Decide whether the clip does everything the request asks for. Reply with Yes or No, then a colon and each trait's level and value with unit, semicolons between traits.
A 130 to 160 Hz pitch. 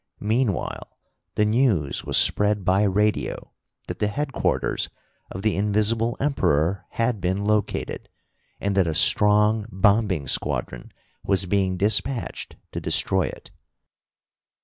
No: low, 105 Hz